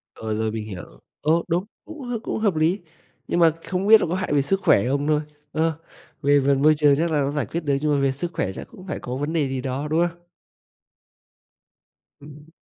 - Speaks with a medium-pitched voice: Yes, medium, 150 Hz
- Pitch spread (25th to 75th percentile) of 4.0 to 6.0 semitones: No, average, 3.6 semitones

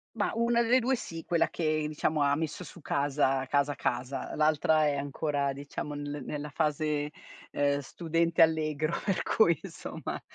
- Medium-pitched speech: Yes, medium, 150 Hz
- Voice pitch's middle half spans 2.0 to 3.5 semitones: Yes, narrow, 2.5 semitones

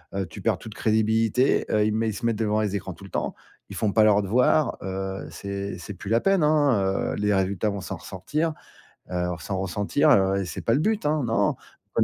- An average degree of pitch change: Yes, average, 3.1 semitones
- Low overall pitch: Yes, low, 105 Hz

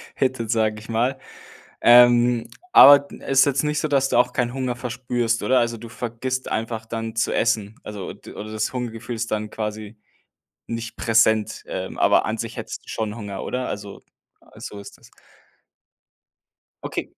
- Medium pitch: No, low, 115 Hz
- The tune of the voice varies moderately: No, narrow, 2.2 semitones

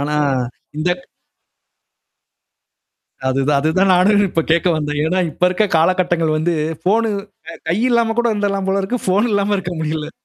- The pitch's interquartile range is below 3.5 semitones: No, average, 4.0 semitones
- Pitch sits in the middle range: Yes, medium, 180 Hz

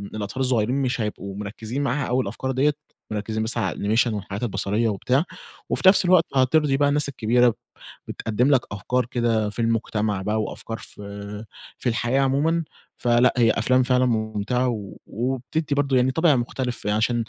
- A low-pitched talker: Yes, low, 120 Hz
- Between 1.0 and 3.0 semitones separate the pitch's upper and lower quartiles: No, average, 3.5 semitones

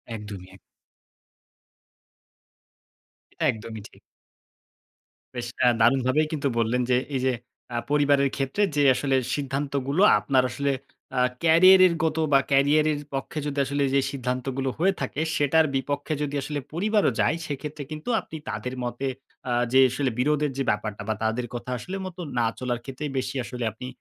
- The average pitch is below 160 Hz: Yes, low, 135 Hz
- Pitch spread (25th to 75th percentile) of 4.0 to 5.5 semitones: No, average, 2.9 semitones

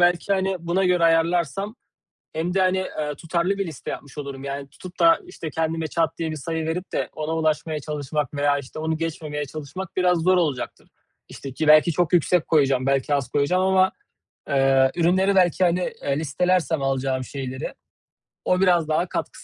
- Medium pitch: Yes, medium, 160 Hz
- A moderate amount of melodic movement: Yes, average, 3.9 semitones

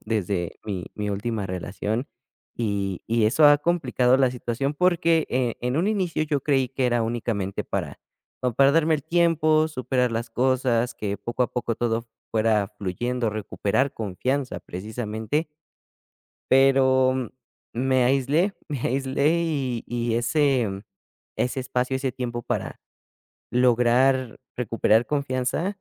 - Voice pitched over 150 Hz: No, low, 125 Hz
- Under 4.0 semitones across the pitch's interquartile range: Yes, average, 3.3 semitones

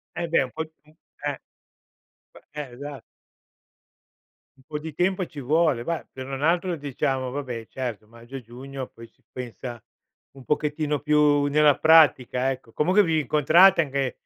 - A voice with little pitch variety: No, average, 3.4 semitones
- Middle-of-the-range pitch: Yes, medium, 145 Hz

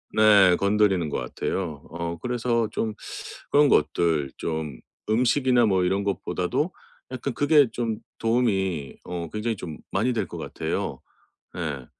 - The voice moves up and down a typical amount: No, wide, 5.8 semitones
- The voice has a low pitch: Yes, low, 100 Hz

